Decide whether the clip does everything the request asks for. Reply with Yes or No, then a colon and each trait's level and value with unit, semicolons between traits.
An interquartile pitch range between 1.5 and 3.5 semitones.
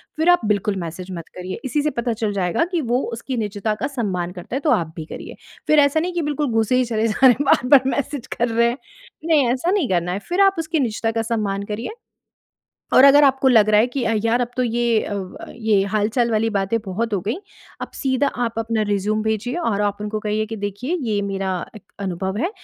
No: average, 4.3 semitones